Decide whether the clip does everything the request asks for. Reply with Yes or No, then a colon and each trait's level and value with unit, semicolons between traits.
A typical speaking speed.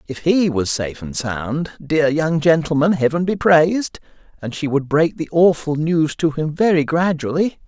Yes: average, 180 wpm